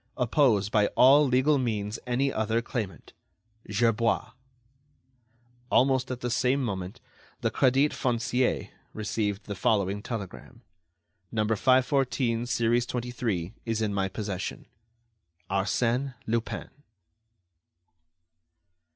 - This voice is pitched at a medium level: No, low, 115 Hz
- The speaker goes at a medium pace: No, slow, 100 wpm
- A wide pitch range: No, average, 3.4 semitones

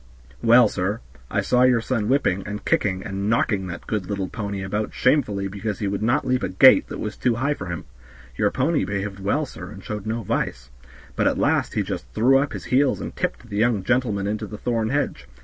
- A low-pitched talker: Yes, low, 105 Hz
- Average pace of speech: No, fast, 220 wpm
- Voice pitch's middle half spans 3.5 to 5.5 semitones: Yes, average, 4.1 semitones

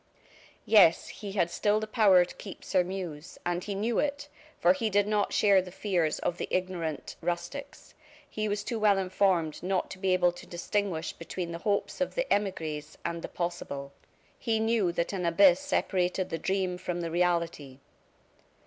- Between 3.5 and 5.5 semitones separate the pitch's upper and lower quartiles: No, average, 3.0 semitones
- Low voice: No, medium, 185 Hz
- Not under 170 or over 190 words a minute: Yes, average, 175 wpm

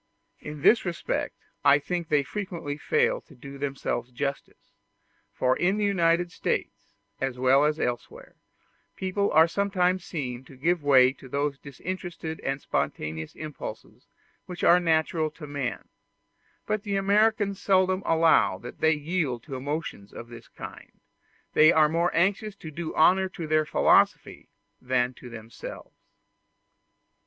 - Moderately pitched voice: Yes, medium, 155 Hz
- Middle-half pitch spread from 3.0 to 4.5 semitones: No, average, 5.0 semitones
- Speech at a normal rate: Yes, average, 145 wpm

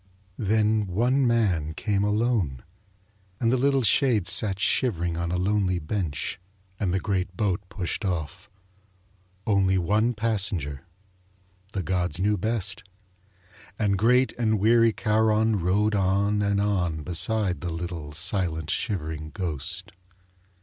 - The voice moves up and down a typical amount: Yes, average, 3.7 semitones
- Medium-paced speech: No, slow, 125 wpm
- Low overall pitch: Yes, low, 100 Hz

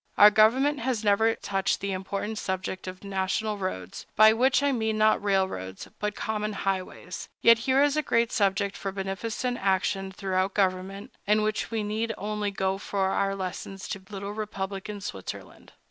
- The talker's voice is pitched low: No, high, 200 Hz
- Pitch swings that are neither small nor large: No, narrow, 2.2 semitones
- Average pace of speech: Yes, average, 165 wpm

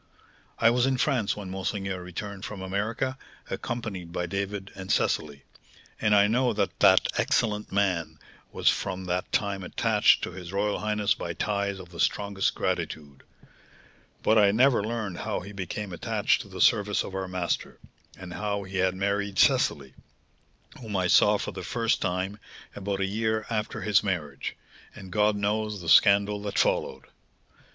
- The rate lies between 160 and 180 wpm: Yes, average, 165 wpm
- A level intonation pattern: Yes, narrow, 2.2 semitones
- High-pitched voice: No, low, 100 Hz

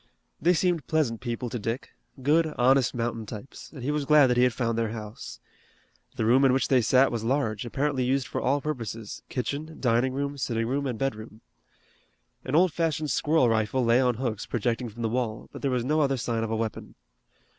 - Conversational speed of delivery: No, fast, 210 wpm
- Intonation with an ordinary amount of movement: Yes, average, 3.5 semitones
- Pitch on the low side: Yes, low, 125 Hz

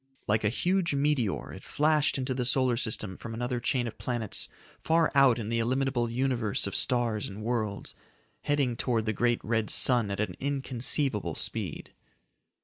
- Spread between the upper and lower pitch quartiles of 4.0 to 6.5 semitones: No, average, 3.4 semitones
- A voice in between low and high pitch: No, low, 120 Hz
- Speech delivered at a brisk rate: No, average, 165 wpm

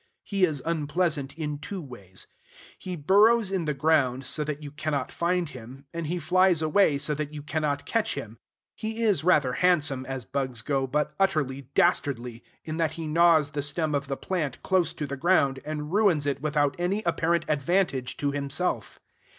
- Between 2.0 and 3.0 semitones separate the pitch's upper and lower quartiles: No, average, 3.8 semitones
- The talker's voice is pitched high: No, medium, 150 Hz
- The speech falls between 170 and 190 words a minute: Yes, average, 185 wpm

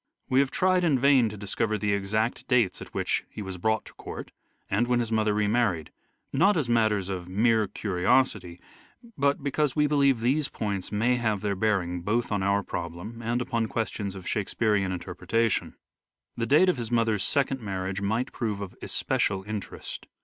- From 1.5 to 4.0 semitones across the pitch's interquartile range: Yes, average, 3.7 semitones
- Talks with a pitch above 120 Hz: No, low, 110 Hz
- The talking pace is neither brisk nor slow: Yes, average, 185 wpm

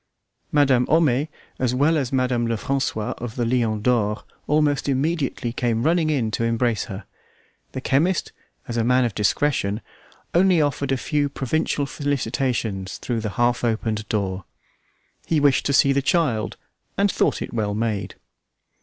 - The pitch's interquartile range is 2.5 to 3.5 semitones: No, average, 4.2 semitones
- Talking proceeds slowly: No, average, 150 wpm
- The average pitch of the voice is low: Yes, low, 125 Hz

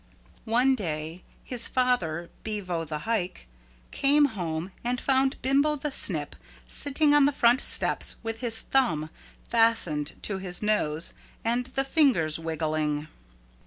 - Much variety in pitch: Yes, wide, 8.3 semitones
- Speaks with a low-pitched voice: No, high, 225 Hz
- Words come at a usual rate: No, slow, 130 wpm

